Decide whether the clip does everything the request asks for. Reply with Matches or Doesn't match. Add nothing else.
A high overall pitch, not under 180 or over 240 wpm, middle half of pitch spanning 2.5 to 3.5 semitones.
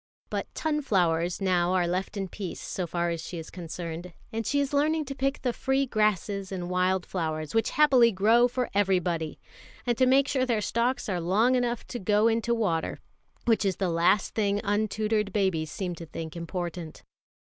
Doesn't match